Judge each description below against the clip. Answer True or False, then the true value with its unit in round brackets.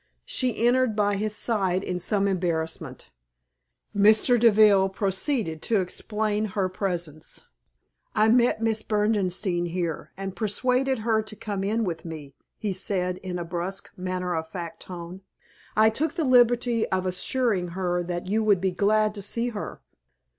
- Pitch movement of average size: True (3.5 semitones)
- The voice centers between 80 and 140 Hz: False (200 Hz)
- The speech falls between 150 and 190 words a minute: True (155 wpm)